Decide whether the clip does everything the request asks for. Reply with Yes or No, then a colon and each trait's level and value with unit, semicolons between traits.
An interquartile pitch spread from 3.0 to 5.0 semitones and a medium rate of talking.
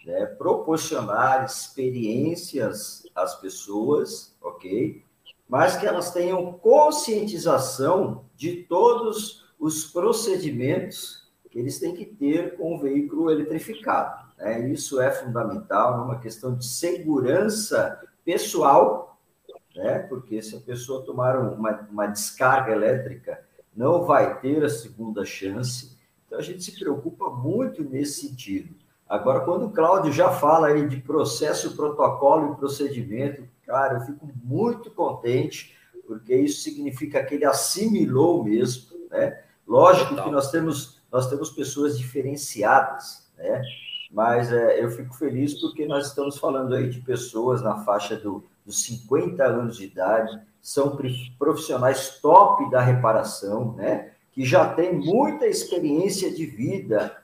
No: wide, 5.5 semitones; average, 130 wpm